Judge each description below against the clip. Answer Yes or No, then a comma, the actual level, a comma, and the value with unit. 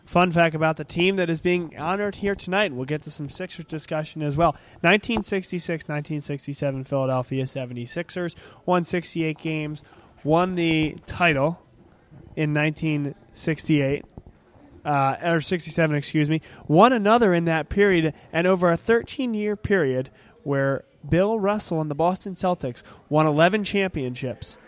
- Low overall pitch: No, medium, 160 Hz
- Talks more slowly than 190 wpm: Yes, average, 140 wpm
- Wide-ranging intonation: No, average, 3.6 semitones